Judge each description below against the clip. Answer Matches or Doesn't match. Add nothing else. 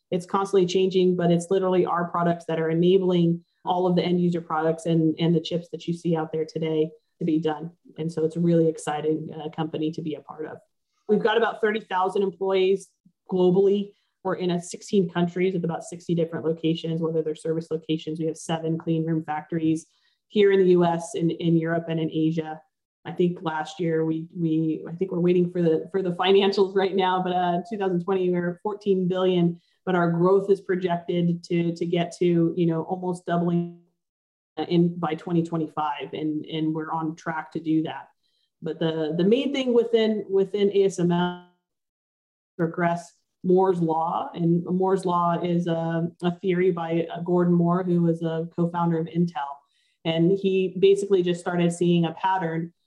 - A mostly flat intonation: Matches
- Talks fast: Doesn't match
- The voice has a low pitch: Doesn't match